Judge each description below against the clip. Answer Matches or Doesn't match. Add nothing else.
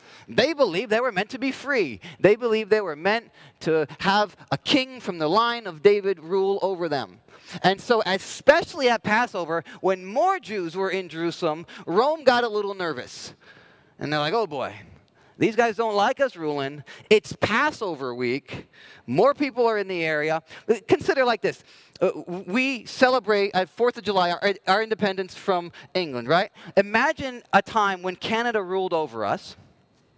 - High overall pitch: Matches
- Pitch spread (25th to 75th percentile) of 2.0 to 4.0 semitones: Doesn't match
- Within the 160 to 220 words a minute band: Matches